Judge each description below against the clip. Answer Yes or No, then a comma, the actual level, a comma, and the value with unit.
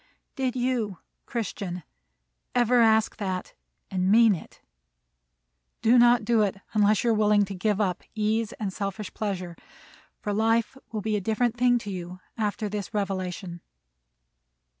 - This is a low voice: No, high, 210 Hz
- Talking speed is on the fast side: No, average, 145 wpm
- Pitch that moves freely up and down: No, average, 2.9 semitones